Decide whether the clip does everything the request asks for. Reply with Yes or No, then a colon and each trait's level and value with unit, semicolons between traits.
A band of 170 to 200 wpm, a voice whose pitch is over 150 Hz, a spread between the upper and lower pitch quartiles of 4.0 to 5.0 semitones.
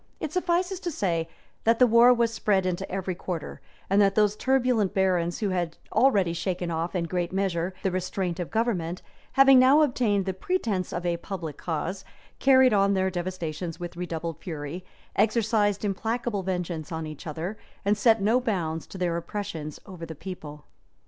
Yes: average, 175 wpm; high, 190 Hz; average, 4.5 semitones